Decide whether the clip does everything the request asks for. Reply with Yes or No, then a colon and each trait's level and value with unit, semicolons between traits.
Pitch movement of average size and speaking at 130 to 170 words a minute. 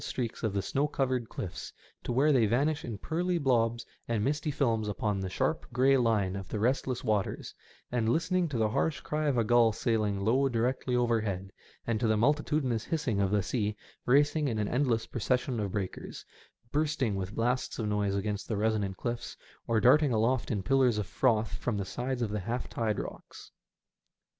No: average, 3.9 semitones; average, 190 wpm